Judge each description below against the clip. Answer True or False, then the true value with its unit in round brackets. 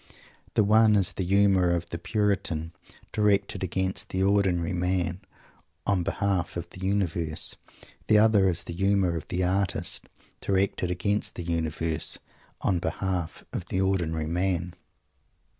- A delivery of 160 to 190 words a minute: False (140 wpm)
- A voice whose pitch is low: True (95 Hz)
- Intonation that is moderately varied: False (2.3 semitones)